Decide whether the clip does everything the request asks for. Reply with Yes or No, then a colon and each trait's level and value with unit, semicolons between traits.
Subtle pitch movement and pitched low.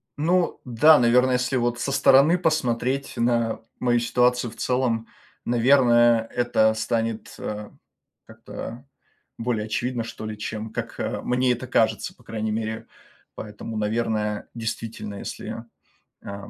Yes: narrow, 2.2 semitones; low, 120 Hz